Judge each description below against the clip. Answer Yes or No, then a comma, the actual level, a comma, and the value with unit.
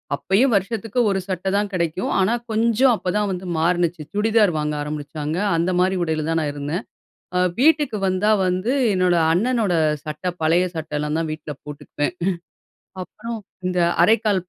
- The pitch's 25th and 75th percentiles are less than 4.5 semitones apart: No, average, 4.8 semitones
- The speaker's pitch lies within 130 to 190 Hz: Yes, medium, 185 Hz